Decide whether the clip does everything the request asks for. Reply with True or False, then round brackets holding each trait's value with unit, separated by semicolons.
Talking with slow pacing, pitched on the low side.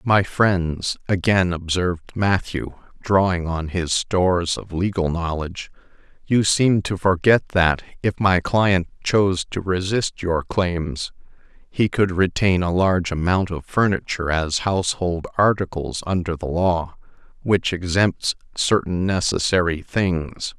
True (130 wpm; 90 Hz)